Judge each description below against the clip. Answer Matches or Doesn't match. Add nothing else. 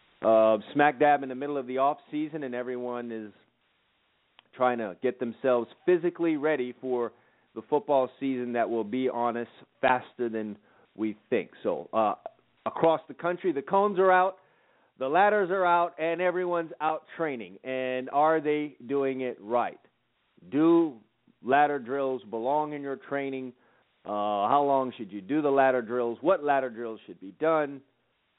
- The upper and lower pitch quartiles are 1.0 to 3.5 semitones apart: Doesn't match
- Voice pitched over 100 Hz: Matches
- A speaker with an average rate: Matches